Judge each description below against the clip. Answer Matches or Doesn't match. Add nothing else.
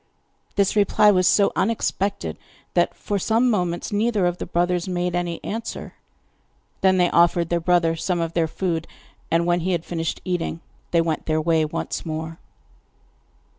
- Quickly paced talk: Doesn't match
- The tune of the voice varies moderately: Doesn't match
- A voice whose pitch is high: Doesn't match